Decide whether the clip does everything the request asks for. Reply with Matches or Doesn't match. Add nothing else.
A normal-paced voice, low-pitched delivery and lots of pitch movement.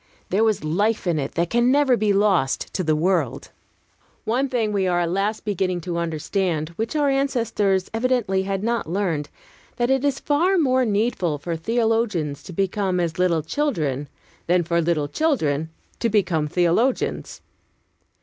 Doesn't match